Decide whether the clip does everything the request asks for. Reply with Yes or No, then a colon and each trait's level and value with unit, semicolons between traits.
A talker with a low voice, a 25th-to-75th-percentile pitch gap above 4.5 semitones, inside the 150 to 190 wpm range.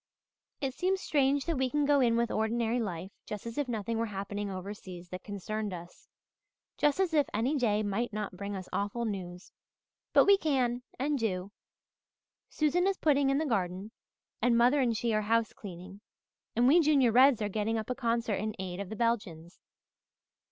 No: high, 225 Hz; average, 4.9 semitones; average, 185 wpm